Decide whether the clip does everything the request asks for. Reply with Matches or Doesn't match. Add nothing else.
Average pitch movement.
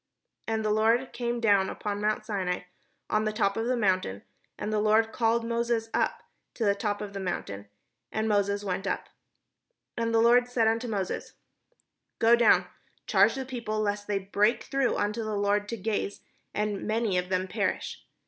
Doesn't match